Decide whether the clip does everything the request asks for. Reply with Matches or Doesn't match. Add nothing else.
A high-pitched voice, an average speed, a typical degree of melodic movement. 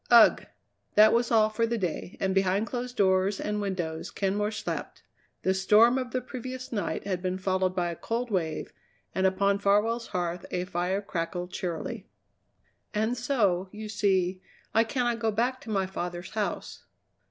Matches